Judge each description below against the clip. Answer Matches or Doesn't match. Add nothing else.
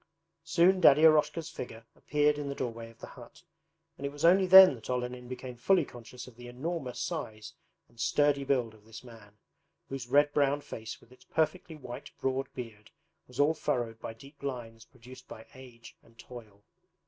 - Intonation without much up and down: Doesn't match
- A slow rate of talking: Doesn't match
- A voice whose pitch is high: Doesn't match